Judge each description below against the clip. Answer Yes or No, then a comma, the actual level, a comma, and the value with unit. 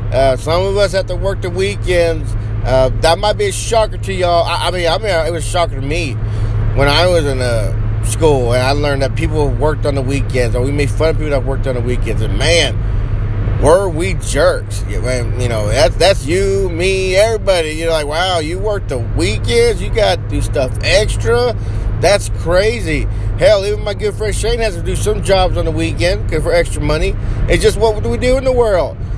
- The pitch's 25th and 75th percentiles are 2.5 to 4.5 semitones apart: Yes, average, 4.0 semitones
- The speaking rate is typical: No, fast, 220 wpm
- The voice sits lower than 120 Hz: Yes, low, 110 Hz